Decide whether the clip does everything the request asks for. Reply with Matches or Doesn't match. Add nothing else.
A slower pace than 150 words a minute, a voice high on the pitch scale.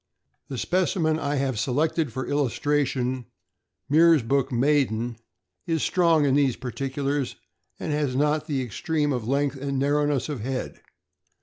Doesn't match